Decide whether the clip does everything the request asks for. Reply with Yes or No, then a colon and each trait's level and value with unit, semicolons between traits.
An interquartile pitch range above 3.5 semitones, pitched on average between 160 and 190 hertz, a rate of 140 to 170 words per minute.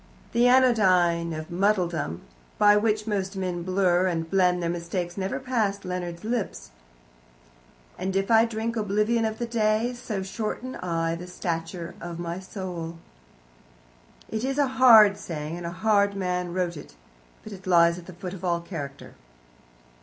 Yes: average, 3.9 semitones; medium, 185 Hz; average, 160 wpm